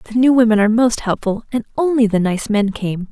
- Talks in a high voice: Yes, high, 225 Hz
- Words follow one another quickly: Yes, fast, 230 wpm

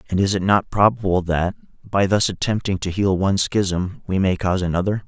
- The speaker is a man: Yes, male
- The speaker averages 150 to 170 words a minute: No, average, 200 wpm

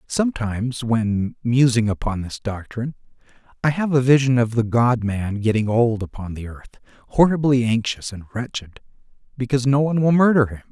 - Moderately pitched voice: No, low, 120 Hz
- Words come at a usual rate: Yes, average, 160 wpm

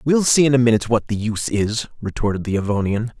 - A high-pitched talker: No, low, 115 Hz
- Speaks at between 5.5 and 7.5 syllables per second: Yes, 6.6 syllables/s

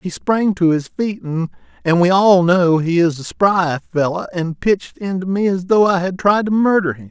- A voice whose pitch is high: No, medium, 175 Hz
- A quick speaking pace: Yes, fast, 220 wpm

